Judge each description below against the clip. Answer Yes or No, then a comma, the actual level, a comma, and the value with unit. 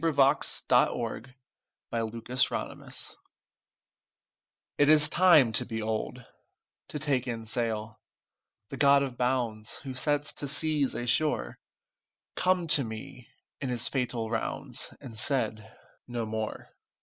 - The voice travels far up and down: No, average, 4.1 semitones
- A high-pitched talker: No, low, 125 Hz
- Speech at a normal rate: No, slow, 125 wpm